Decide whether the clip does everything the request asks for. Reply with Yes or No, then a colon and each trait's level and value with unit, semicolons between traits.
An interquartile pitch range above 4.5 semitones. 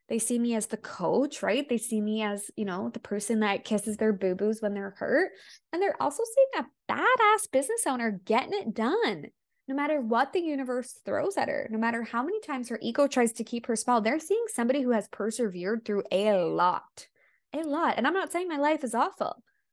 Yes: average, 5.2 semitones